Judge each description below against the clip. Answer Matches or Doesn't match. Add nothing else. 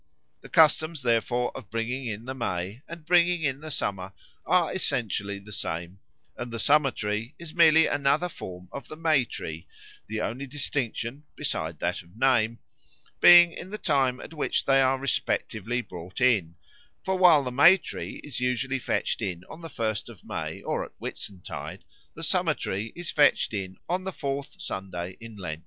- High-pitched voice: Doesn't match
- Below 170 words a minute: Doesn't match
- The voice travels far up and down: Matches